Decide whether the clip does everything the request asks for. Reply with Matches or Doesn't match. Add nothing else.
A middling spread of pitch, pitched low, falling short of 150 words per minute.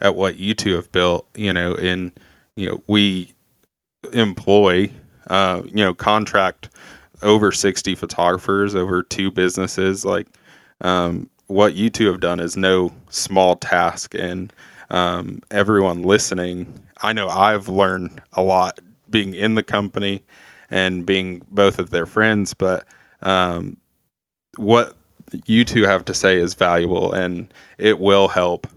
Doesn't match